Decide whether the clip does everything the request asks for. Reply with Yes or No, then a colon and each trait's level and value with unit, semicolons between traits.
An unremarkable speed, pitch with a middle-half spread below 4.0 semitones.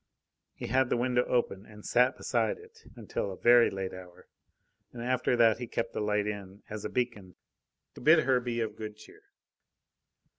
Yes: average, 185 wpm; average, 3.0 semitones